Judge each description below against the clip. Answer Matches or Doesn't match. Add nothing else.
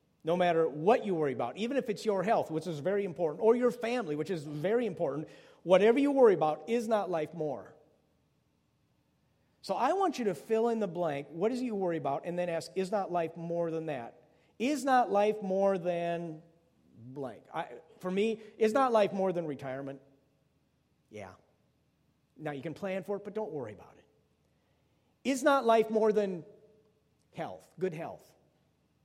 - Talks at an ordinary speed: Matches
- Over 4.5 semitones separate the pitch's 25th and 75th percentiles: Matches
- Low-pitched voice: Doesn't match